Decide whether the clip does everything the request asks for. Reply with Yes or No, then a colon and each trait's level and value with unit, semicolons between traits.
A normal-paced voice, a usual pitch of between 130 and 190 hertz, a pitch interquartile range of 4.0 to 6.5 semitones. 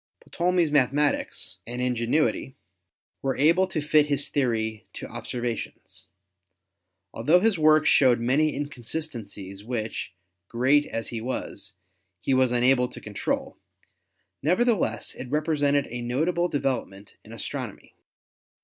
No: slow, 120 wpm; low, 135 Hz; average, 4.4 semitones